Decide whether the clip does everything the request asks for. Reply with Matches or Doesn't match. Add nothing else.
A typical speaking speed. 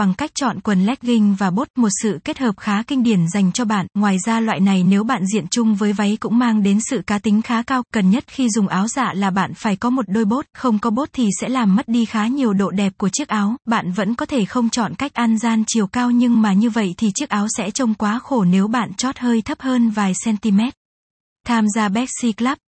Doesn't match